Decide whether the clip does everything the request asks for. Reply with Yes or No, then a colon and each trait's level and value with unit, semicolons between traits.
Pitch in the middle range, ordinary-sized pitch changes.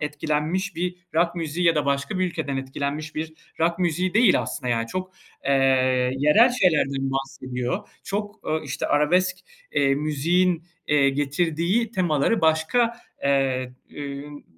Yes: medium, 155 Hz; average, 4.4 semitones